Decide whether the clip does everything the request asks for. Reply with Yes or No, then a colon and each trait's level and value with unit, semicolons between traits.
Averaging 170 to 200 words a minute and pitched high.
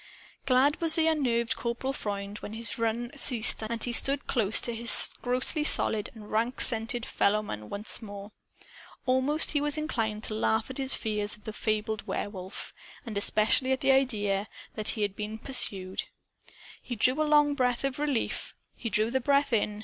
Yes: average, 180 wpm; high, 230 Hz